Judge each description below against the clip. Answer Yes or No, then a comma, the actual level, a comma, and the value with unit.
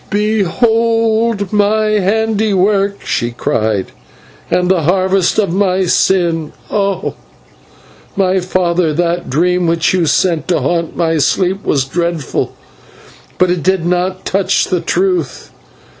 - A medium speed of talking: No, slow, 120 wpm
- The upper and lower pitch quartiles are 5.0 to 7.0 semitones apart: No, average, 2.8 semitones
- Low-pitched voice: No, medium, 185 Hz